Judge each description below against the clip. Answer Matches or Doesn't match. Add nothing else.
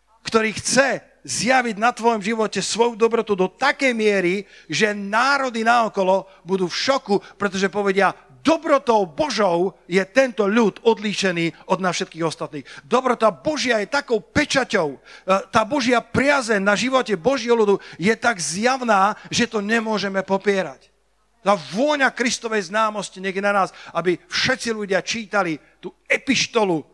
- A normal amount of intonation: Matches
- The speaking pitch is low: Doesn't match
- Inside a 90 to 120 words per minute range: Doesn't match